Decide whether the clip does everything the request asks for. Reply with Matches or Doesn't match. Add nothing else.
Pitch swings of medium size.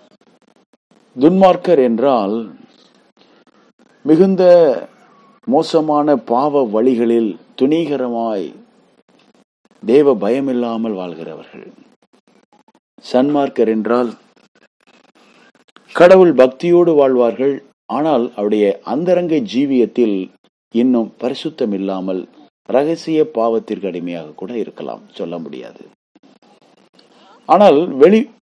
Doesn't match